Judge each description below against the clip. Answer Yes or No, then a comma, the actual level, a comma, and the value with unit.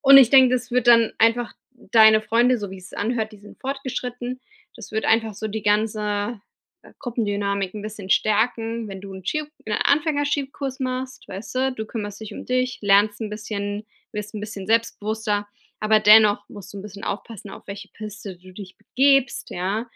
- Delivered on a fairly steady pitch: No, average, 3.2 semitones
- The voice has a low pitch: No, high, 220 Hz